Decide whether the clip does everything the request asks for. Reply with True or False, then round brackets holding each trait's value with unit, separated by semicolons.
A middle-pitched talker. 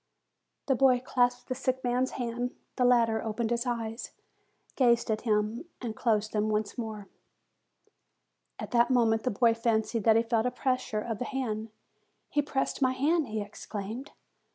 False (235 Hz)